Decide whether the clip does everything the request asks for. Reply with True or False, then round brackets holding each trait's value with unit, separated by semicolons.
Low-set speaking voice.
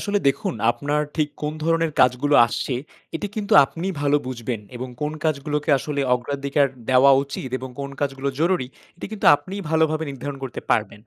False (145 Hz)